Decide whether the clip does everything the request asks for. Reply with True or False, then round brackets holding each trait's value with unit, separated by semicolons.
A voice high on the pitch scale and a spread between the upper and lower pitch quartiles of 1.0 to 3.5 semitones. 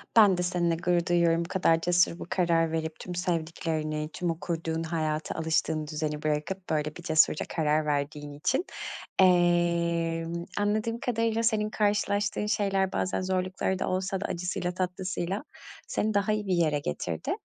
False (175 Hz; 2.9 semitones)